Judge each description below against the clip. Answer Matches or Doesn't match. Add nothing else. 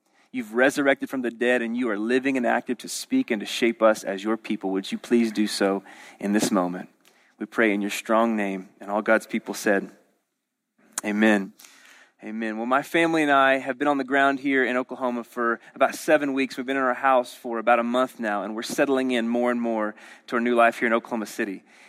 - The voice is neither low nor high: Doesn't match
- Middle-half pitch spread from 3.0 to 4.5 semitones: Matches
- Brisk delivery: Matches